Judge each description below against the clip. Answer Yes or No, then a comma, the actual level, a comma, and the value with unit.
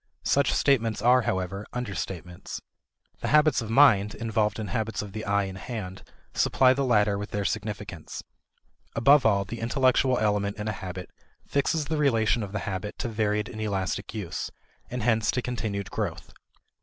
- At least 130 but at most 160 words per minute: No, average, 170 wpm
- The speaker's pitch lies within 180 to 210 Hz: No, low, 110 Hz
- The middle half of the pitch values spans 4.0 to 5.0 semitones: No, average, 3.5 semitones